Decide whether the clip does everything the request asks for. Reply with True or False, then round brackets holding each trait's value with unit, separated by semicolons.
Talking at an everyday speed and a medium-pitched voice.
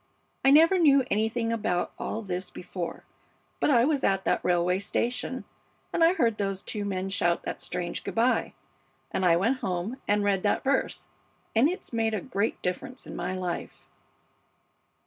False (170 wpm; 210 Hz)